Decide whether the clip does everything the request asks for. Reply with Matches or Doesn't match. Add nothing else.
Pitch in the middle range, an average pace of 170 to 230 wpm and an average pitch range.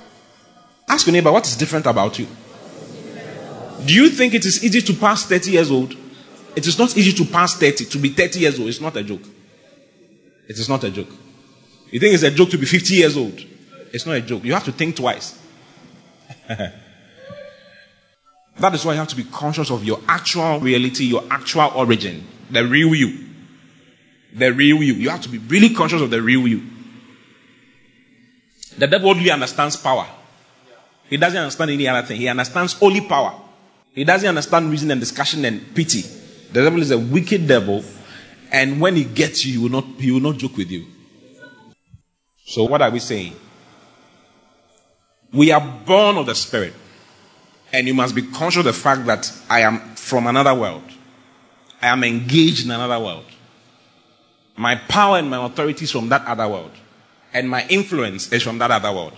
Doesn't match